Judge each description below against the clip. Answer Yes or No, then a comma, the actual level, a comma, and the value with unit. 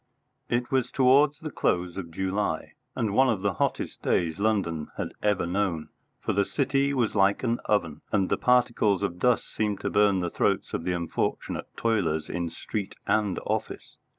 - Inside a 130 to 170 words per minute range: No, average, 180 wpm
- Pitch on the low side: Yes, low, 100 Hz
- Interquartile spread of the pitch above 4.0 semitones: Yes, average, 5.1 semitones